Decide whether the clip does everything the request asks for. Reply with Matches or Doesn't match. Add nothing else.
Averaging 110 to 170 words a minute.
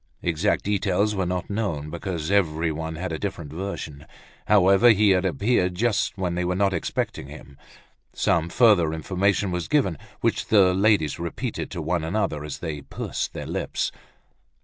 Matches